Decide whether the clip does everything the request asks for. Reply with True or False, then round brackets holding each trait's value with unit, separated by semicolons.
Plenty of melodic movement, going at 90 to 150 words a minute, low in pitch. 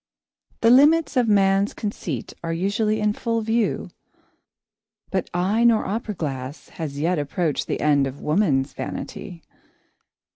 False (6.4 semitones; 140 wpm; 195 Hz)